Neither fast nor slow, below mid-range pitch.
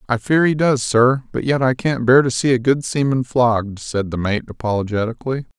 No: fast, 215 wpm; low, 125 Hz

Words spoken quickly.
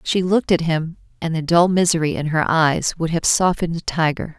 Yes: fast, 220 wpm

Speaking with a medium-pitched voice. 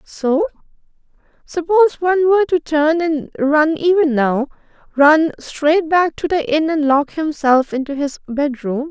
No: very high, 310 Hz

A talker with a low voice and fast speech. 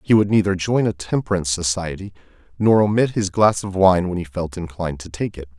Yes: very low, 95 Hz; fast, 215 wpm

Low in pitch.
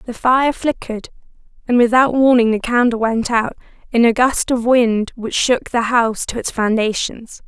No: high, 235 Hz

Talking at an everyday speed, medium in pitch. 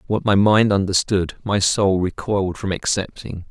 No: average, 155 wpm; low, 100 Hz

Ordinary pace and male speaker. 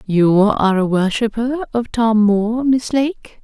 No: average, 155 wpm; female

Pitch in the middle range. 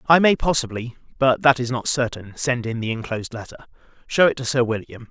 No: low, 125 Hz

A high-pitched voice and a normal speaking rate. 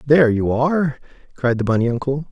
No: low, 135 Hz; average, 180 wpm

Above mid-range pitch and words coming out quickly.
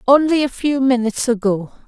No: very high, 250 Hz; average, 160 wpm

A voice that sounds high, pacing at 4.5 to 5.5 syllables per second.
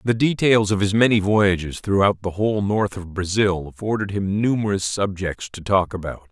No: low, 100 Hz; 5.0 syllables/s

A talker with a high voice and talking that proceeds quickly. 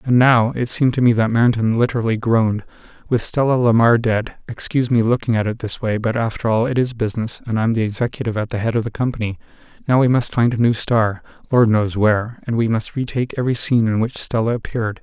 No: low, 115 Hz; fast, 210 wpm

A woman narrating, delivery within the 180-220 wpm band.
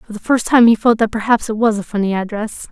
No: female; fast, 285 wpm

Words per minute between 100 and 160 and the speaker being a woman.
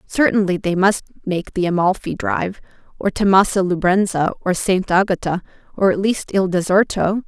Yes: average, 155 wpm; female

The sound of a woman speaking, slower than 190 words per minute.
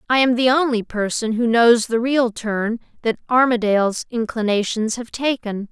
Yes: female; average, 160 wpm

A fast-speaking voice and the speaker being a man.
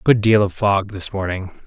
Yes: fast, 215 wpm; male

